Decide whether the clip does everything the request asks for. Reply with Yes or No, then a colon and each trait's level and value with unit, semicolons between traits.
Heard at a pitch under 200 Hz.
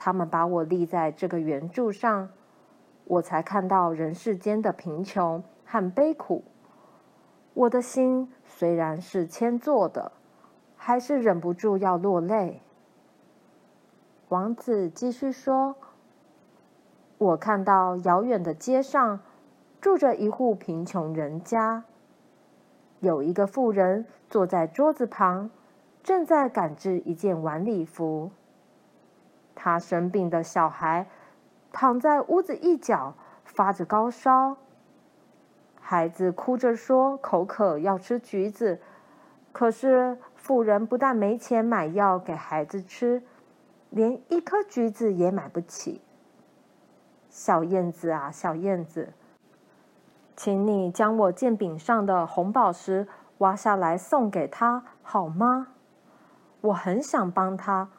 No: high, 205 Hz